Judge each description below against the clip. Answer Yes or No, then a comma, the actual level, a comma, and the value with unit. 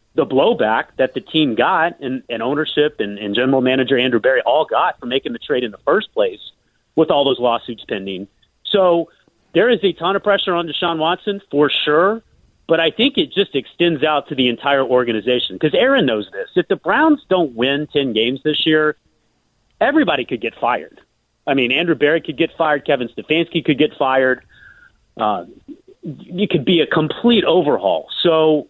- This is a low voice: No, medium, 155 Hz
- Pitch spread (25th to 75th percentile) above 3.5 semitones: Yes, wide, 5.6 semitones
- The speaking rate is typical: Yes, average, 190 wpm